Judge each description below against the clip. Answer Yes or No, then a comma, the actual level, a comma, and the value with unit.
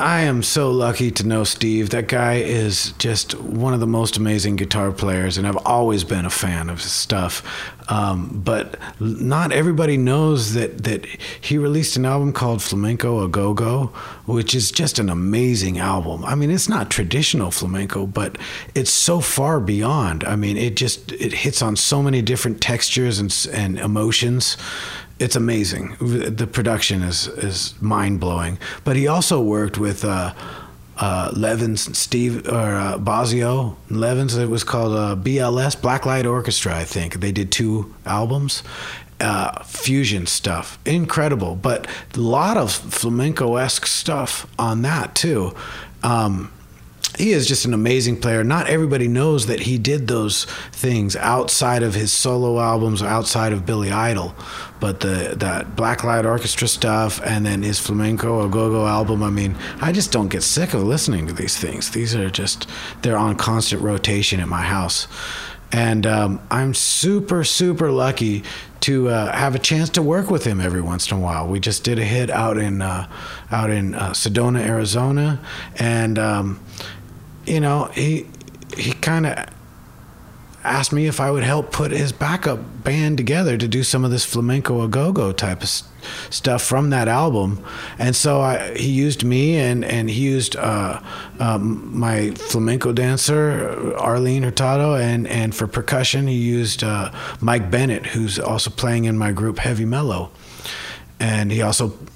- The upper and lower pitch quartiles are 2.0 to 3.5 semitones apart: No, average, 4.1 semitones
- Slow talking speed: No, average, 170 wpm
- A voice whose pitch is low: Yes, low, 115 Hz